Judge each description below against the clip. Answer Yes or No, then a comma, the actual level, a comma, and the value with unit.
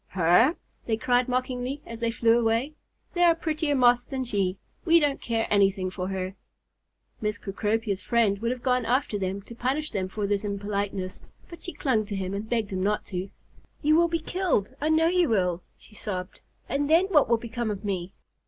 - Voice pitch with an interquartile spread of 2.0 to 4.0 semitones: No, average, 5.1 semitones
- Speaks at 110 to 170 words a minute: No, average, 200 wpm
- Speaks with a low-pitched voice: No, high, 225 Hz